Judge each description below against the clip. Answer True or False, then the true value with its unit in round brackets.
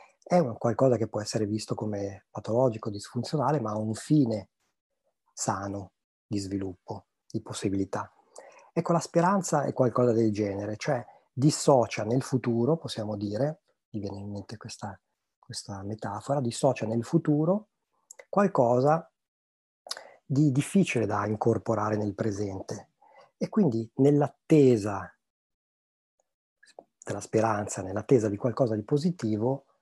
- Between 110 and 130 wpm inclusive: True (120 wpm)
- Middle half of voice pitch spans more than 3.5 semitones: True (5.0 semitones)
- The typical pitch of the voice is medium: False (115 Hz)